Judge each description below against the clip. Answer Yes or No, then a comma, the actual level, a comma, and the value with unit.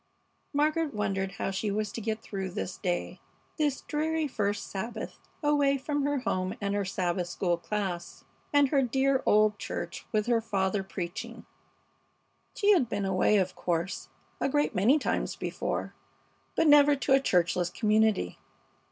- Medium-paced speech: Yes, average, 150 wpm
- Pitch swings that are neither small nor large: No, wide, 6.6 semitones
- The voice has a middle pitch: No, high, 210 Hz